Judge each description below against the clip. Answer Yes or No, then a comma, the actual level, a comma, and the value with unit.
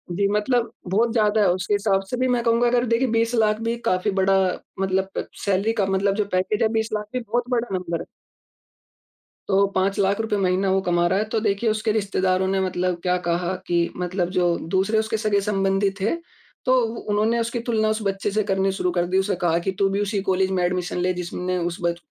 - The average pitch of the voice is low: No, high, 195 Hz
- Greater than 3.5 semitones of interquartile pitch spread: No, average, 3.0 semitones